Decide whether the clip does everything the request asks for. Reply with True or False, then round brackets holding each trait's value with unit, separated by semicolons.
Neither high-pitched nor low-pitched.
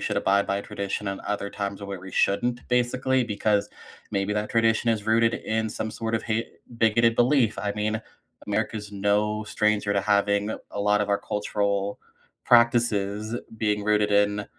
False (105 Hz)